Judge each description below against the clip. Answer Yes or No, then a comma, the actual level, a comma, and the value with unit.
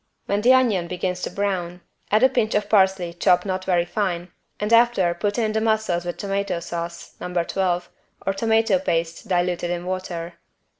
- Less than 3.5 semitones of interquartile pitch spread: Yes, average, 3.0 semitones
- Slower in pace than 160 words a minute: No, average, 180 wpm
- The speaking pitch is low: No, medium, 185 Hz